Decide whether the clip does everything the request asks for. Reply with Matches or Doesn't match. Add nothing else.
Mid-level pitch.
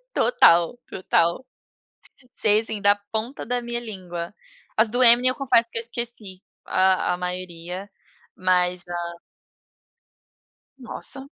Doesn't match